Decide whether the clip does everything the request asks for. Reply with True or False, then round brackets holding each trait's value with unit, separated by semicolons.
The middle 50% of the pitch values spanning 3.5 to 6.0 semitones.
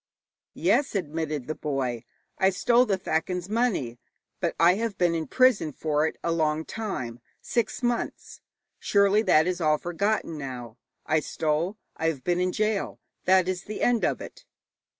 True (4.9 semitones)